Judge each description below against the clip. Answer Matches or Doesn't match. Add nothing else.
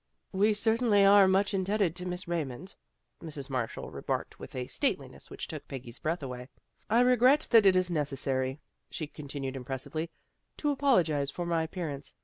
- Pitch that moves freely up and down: Matches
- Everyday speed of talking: Matches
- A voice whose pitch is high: Doesn't match